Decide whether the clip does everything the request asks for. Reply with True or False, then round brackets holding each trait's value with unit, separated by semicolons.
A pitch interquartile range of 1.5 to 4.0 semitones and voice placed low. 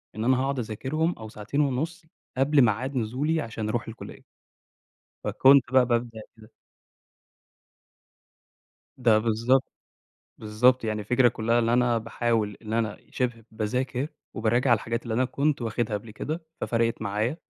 True (3.0 semitones; 120 Hz)